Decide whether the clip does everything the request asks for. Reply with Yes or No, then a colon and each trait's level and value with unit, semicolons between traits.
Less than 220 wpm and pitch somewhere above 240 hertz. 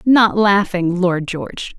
No: slow, 135 wpm; high, 190 Hz